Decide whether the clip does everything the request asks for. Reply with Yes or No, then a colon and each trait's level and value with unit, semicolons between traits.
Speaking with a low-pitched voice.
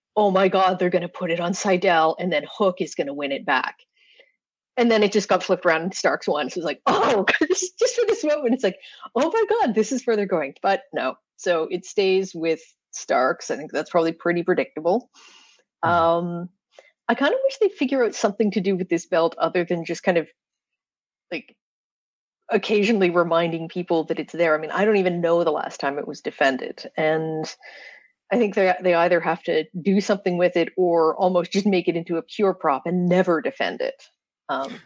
No: medium, 185 Hz